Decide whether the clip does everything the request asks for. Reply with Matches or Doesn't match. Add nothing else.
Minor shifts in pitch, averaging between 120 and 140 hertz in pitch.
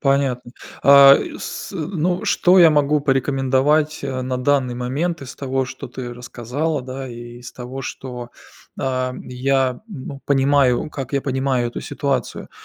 Matches